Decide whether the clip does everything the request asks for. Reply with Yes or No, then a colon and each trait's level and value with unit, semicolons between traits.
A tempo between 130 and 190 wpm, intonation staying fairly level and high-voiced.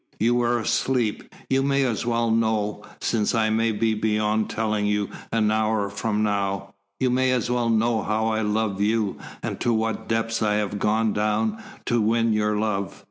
No: average, 185 wpm; narrow, 1.6 semitones; low, 110 Hz